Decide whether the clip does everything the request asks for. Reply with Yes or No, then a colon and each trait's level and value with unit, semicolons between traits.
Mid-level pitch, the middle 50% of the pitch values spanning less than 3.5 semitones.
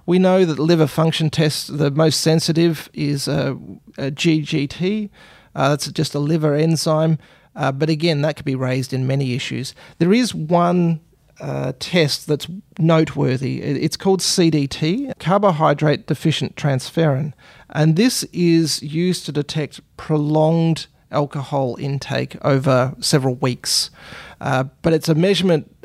Yes: medium, 155 Hz; average, 3.0 semitones